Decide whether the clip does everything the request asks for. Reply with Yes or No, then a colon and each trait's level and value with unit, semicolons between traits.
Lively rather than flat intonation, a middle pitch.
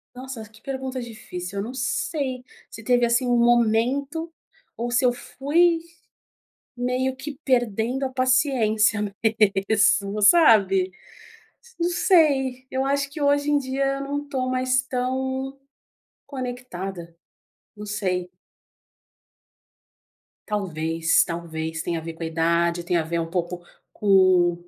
No: wide, 6.0 semitones; high, 245 Hz